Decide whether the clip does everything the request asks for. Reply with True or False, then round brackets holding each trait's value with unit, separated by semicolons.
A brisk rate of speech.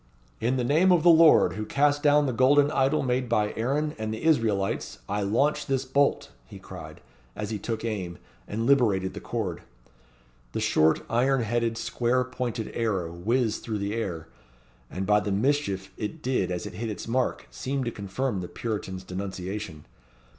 False (175 wpm)